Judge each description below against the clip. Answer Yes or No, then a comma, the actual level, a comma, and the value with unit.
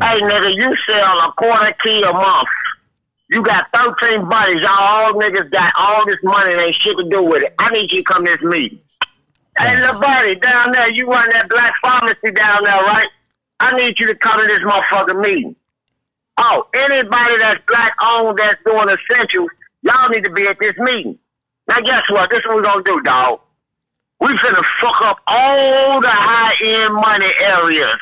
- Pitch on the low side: No, high, 220 Hz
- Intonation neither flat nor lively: Yes, average, 3.1 semitones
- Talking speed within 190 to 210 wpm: Yes, average, 195 wpm